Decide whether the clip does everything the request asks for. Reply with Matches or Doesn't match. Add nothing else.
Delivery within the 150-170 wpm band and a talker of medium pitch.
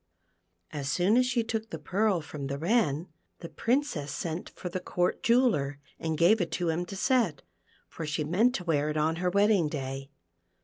Doesn't match